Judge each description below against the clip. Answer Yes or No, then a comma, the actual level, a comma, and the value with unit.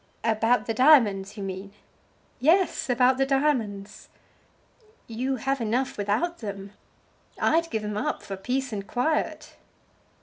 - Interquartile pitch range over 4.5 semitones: Yes, average, 4.9 semitones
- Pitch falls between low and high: No, high, 235 Hz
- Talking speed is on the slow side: Yes, slow, 130 wpm